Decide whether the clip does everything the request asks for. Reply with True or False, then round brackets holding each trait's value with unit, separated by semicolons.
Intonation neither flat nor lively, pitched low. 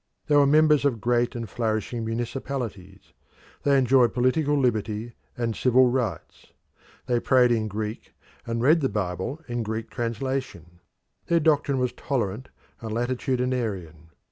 True (3.2 semitones; 120 Hz)